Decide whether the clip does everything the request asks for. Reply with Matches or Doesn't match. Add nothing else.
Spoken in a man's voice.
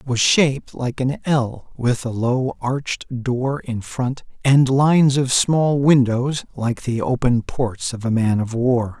Matches